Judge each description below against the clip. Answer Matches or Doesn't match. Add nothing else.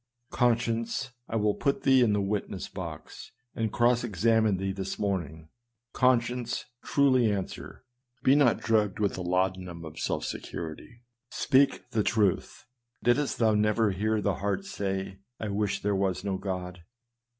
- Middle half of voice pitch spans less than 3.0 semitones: Doesn't match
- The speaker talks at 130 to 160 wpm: Matches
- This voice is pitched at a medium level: Doesn't match